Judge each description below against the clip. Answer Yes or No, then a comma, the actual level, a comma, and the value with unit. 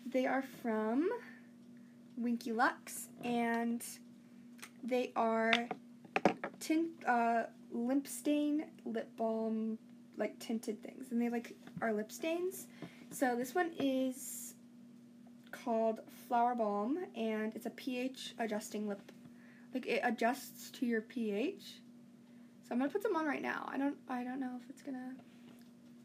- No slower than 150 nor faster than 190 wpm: No, slow, 135 wpm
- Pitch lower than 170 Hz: No, high, 240 Hz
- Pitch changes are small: Yes, narrow, 1.7 semitones